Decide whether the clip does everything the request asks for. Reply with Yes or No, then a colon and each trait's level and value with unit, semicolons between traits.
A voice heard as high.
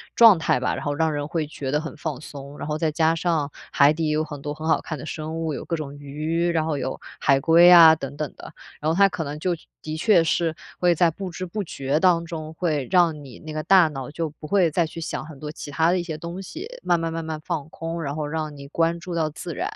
No: medium, 160 Hz